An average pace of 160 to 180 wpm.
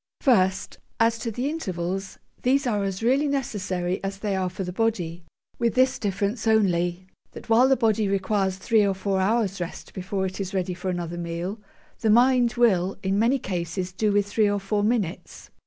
No: average, 190 wpm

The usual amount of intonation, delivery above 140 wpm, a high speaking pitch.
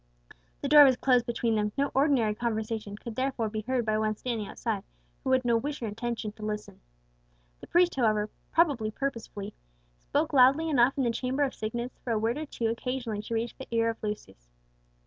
Yes: average, 3.4 semitones; average, 200 wpm; high, 235 Hz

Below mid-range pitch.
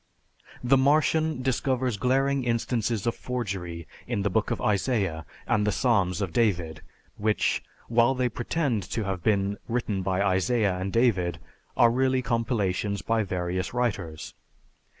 Yes: low, 110 Hz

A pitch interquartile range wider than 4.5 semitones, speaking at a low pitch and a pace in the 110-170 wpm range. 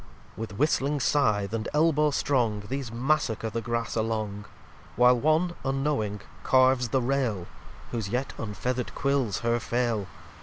No: average, 3.8 semitones; low, 120 Hz; average, 140 wpm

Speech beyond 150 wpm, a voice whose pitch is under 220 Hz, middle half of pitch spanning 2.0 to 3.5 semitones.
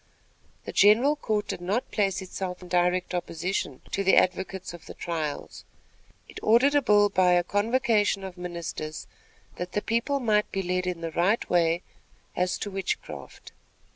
Yes: average, 165 wpm; medium, 185 Hz; average, 2.9 semitones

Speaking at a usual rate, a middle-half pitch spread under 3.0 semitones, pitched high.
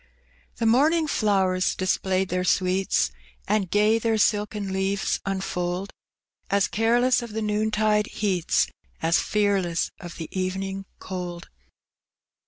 No: slow, 115 wpm; narrow, 2.5 semitones; high, 195 Hz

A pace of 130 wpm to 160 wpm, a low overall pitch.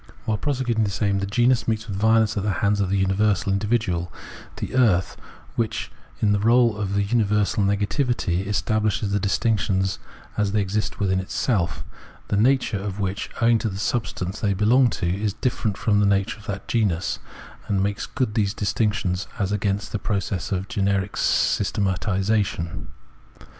No: average, 170 wpm; low, 100 Hz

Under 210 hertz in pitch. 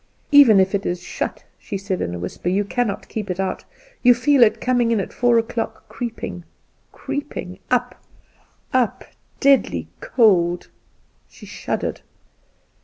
No: high, 220 Hz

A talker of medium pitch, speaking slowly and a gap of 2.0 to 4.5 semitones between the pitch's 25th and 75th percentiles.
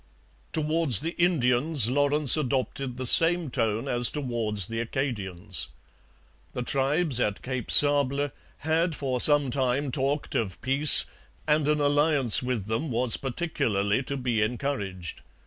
No: low, 130 Hz; slow, 130 wpm; average, 3.9 semitones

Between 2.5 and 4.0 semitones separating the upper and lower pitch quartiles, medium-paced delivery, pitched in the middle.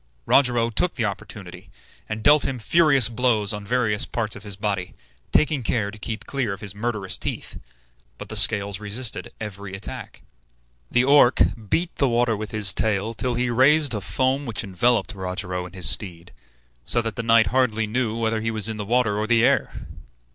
No: average, 3.2 semitones; average, 190 wpm; low, 110 Hz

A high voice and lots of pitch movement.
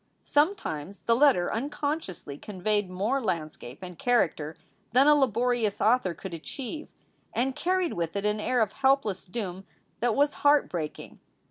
Yes: high, 220 Hz; wide, 7.0 semitones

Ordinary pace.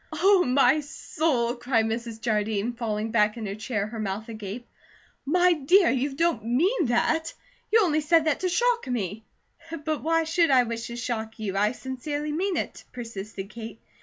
Yes: average, 175 wpm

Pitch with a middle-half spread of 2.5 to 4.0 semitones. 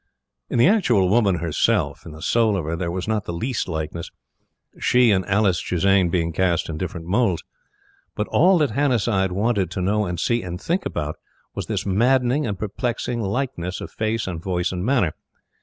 No: average, 5.2 semitones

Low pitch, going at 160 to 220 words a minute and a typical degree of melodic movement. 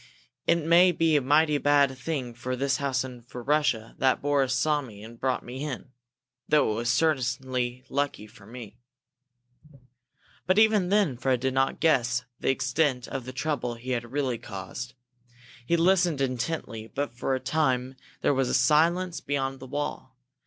Yes: low, 130 Hz; average, 165 wpm; average, 3.3 semitones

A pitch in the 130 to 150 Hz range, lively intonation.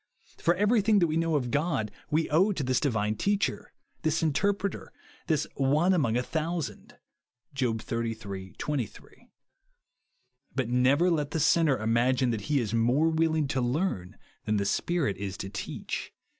Yes: medium, 140 Hz; wide, 6.1 semitones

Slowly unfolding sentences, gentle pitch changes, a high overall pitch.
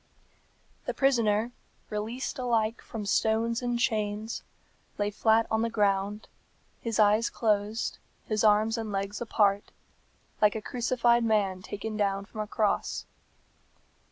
Yes: slow, 125 wpm; narrow, 1.8 semitones; high, 215 Hz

